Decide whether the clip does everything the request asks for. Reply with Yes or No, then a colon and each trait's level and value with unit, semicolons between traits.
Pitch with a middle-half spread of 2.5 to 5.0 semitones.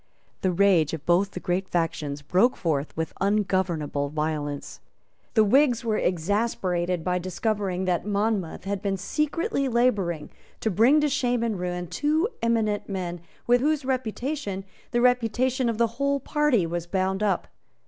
No: wide, 5.4 semitones